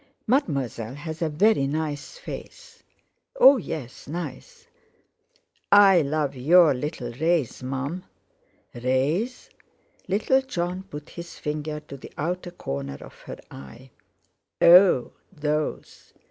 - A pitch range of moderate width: Yes, average, 4.9 semitones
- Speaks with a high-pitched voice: No, medium, 155 Hz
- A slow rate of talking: Yes, slow, 110 wpm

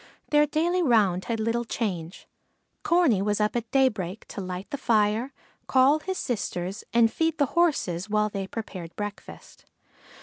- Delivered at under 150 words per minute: No, average, 155 wpm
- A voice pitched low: No, high, 225 Hz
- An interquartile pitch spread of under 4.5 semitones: No, wide, 5.5 semitones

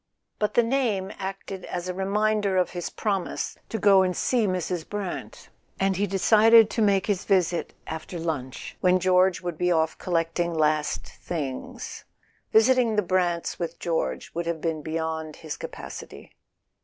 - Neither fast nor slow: Yes, average, 155 wpm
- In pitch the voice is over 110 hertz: Yes, medium, 185 Hz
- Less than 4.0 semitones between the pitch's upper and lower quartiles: Yes, average, 3.4 semitones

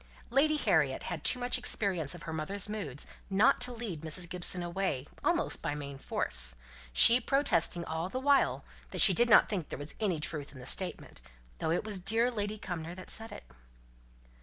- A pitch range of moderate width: No, wide, 5.9 semitones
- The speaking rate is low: No, average, 190 wpm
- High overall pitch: No, medium, 180 Hz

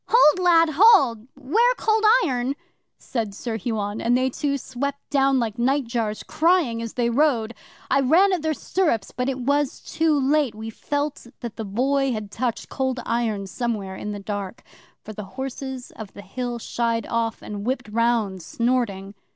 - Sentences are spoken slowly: No, average, 170 wpm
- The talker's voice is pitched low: No, high, 245 Hz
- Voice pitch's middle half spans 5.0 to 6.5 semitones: No, average, 4.1 semitones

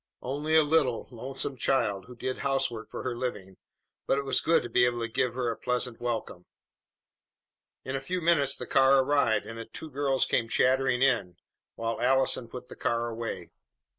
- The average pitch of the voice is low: Yes, low, 125 Hz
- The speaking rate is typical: Yes, average, 190 wpm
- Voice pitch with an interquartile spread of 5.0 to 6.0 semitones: No, average, 2.8 semitones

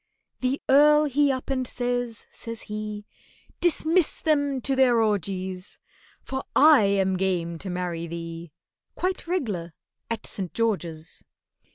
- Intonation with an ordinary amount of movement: No, wide, 6.8 semitones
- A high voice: Yes, high, 225 Hz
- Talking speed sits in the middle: No, slow, 130 wpm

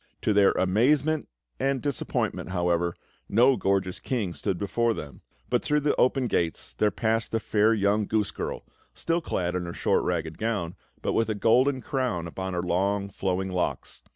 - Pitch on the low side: Yes, low, 100 Hz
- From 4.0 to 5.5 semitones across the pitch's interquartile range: Yes, average, 4.8 semitones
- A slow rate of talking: No, average, 175 wpm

